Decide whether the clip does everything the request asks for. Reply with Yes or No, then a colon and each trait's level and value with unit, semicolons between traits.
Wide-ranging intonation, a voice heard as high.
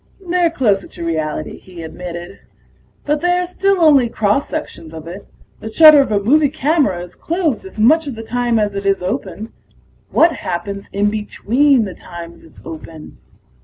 Yes: wide, 8.8 semitones; high, 215 Hz